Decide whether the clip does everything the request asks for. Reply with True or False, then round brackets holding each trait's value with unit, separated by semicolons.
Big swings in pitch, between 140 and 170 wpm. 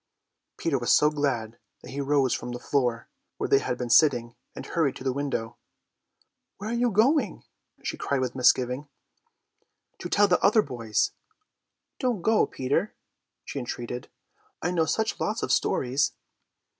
True (6.6 semitones; 155 wpm)